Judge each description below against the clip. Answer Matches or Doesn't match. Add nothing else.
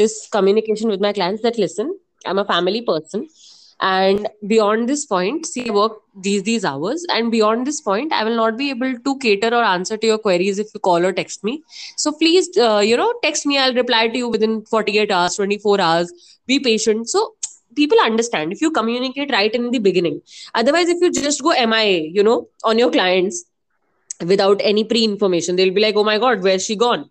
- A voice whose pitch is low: Doesn't match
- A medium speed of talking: Doesn't match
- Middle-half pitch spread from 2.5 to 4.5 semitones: Matches